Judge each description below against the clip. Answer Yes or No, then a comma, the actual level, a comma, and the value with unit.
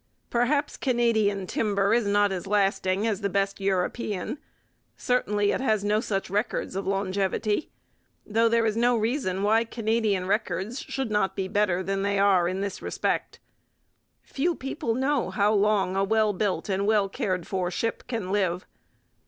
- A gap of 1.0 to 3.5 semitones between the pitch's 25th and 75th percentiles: Yes, average, 2.7 semitones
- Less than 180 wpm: Yes, average, 160 wpm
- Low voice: No, high, 205 Hz